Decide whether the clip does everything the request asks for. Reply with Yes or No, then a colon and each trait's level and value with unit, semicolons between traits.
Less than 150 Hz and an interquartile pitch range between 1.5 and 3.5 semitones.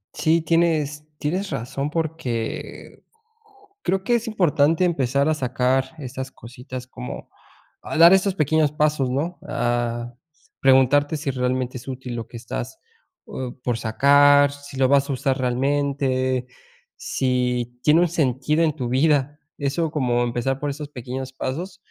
Yes: medium, 140 Hz; average, 3.2 semitones